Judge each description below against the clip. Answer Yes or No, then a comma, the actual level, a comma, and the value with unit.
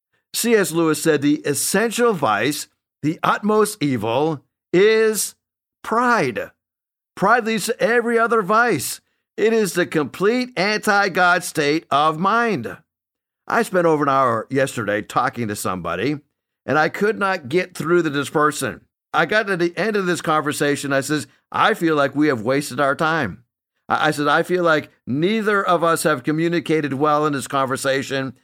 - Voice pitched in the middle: Yes, medium, 155 Hz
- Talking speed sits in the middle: Yes, average, 160 wpm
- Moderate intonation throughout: No, wide, 6.0 semitones